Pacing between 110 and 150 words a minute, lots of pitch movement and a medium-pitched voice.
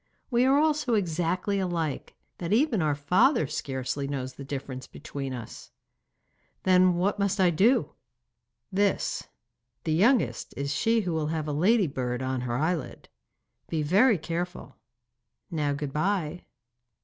Yes: average, 140 wpm; wide, 6.0 semitones; medium, 165 Hz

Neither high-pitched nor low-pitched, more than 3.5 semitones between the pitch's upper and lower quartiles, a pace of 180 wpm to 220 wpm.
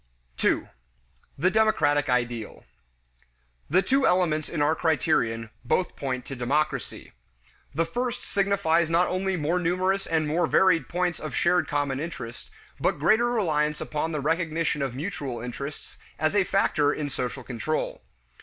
No: medium, 155 Hz; average, 4.4 semitones; average, 145 wpm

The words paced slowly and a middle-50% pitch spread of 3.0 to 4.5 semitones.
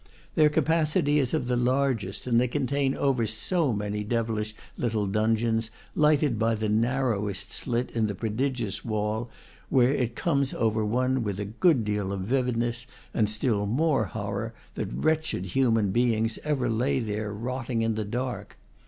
No: average, 160 wpm; average, 3.6 semitones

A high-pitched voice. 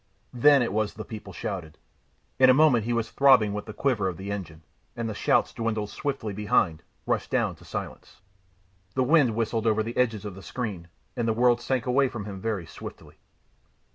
No: low, 110 Hz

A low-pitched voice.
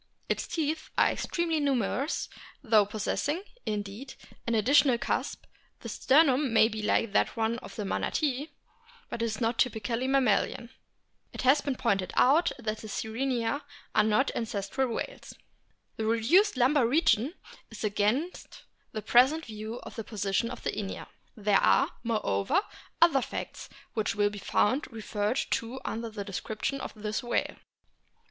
No: high, 230 Hz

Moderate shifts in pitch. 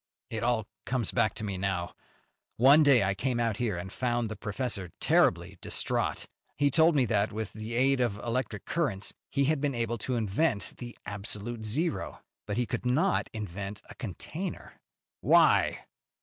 Yes: average, 4.2 semitones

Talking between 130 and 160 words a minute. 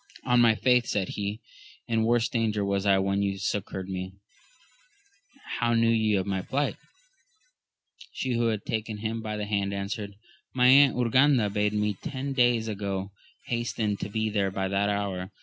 No: average, 170 wpm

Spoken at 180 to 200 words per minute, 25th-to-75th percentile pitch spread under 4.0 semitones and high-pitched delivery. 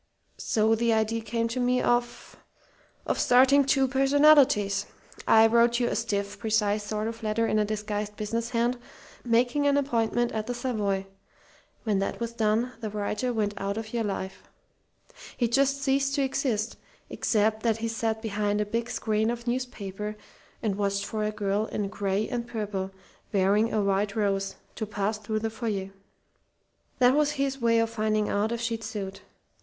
No: average, 170 wpm; narrow, 2.5 semitones; high, 220 Hz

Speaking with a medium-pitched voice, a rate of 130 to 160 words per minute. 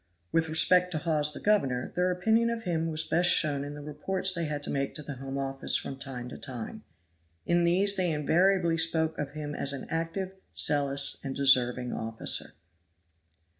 No: medium, 155 Hz; average, 185 wpm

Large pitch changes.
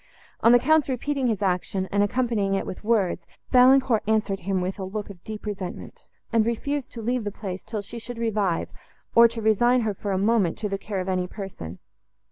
No: average, 3.4 semitones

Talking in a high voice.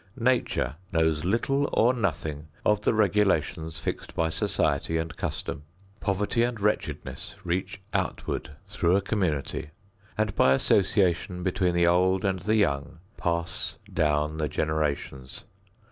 No: very low, 90 Hz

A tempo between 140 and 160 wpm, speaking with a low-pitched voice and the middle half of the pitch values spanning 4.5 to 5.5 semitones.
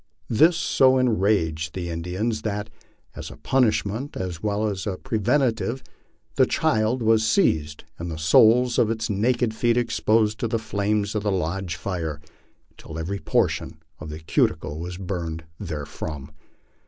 Yes: average, 150 wpm; low, 105 Hz; average, 5.1 semitones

